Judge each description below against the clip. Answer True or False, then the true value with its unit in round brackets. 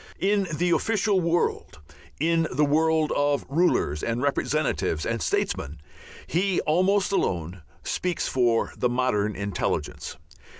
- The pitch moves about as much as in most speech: False (7.3 semitones)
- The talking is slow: True (120 wpm)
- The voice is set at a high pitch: False (150 Hz)